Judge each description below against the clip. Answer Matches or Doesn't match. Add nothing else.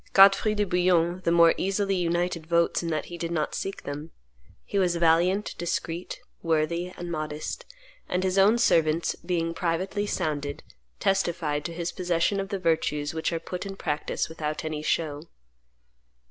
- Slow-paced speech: Doesn't match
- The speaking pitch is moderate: Matches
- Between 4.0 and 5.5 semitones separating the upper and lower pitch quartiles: Doesn't match